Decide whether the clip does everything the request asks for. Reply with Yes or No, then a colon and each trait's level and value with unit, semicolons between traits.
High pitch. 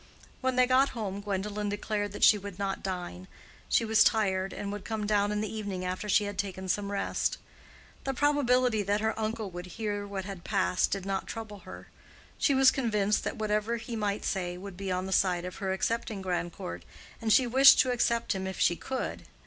Yes: high, 205 Hz